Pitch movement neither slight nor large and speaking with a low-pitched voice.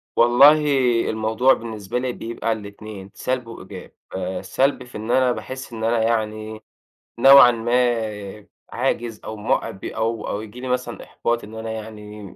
No: narrow, 2.3 semitones; low, 115 Hz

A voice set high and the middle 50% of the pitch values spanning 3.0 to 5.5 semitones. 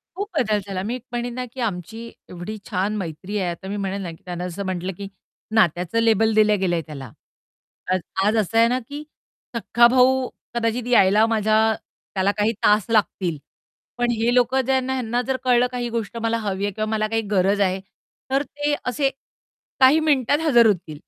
Yes: high, 220 Hz; average, 4.1 semitones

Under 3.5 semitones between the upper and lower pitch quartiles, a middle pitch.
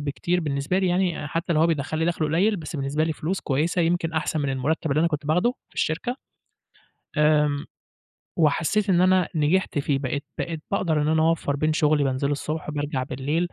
Yes: average, 2.8 semitones; medium, 155 Hz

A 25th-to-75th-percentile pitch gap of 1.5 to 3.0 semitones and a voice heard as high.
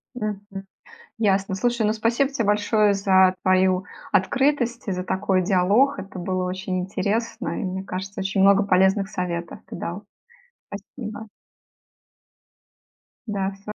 Yes: narrow, 2.4 semitones; high, 195 Hz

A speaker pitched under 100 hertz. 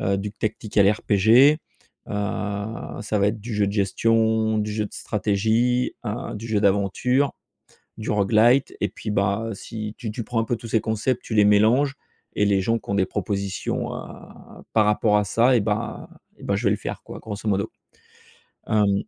No: low, 105 Hz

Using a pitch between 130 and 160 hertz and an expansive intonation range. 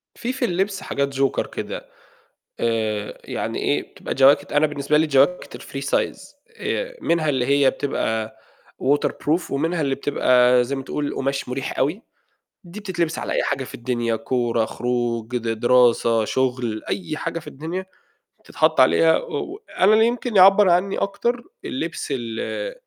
Yes: medium, 140 Hz; wide, 6.2 semitones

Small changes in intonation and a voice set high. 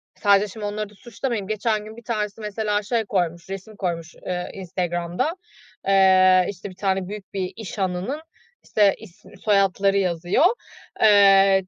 Yes: narrow, 2.3 semitones; high, 195 Hz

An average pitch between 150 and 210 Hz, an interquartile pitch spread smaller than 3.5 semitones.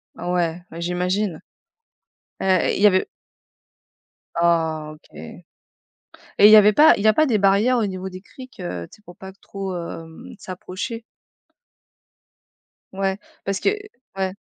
Yes: high, 190 Hz; average, 2.8 semitones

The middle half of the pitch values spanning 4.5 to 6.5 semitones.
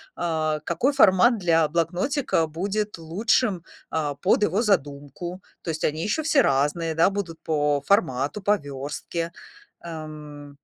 Yes: average, 4.9 semitones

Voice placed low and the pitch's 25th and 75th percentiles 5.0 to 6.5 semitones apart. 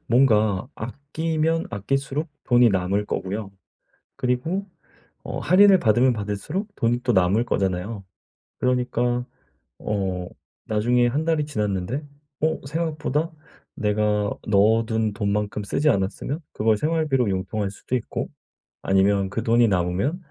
Yes: low, 115 Hz; wide, 5.6 semitones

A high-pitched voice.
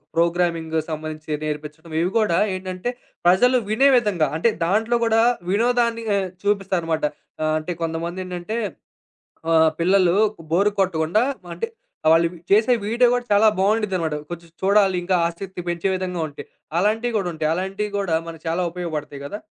No: medium, 180 Hz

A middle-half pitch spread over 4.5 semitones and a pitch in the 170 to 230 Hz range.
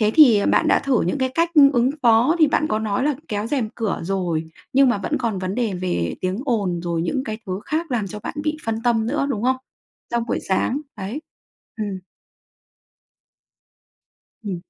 Yes: average, 5.2 semitones; high, 225 Hz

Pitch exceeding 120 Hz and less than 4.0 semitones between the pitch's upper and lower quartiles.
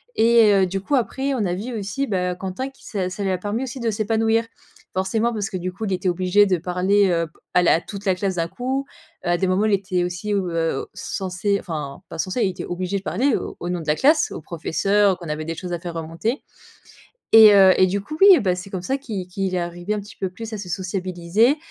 Yes: high, 190 Hz; average, 3.3 semitones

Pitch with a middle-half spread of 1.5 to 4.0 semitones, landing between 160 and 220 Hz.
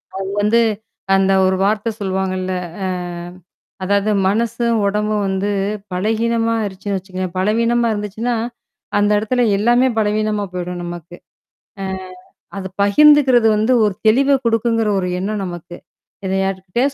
Yes: average, 3.2 semitones; high, 210 Hz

